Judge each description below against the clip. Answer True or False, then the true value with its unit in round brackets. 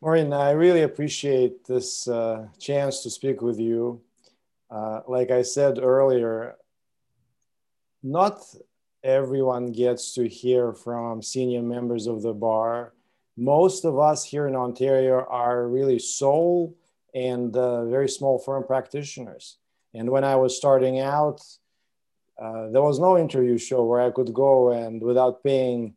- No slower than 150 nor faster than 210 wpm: False (140 wpm)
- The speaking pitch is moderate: False (130 Hz)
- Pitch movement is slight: True (2.3 semitones)